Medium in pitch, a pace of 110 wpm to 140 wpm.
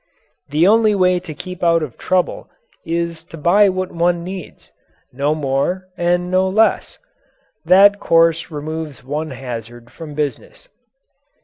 Yes: medium, 170 Hz; slow, 135 wpm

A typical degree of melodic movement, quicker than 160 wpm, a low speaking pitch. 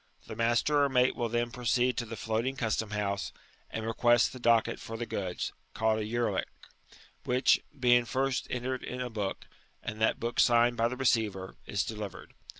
No: narrow, 2.1 semitones; average, 180 wpm; low, 120 Hz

